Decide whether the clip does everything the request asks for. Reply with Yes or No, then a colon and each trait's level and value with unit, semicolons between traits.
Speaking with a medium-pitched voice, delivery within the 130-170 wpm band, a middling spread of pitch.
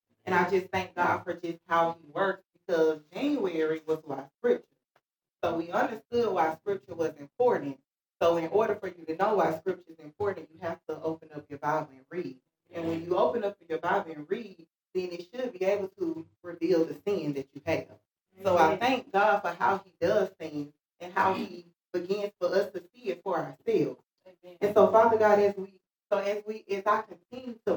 No: medium, 180 Hz; fast, 205 wpm; average, 3.9 semitones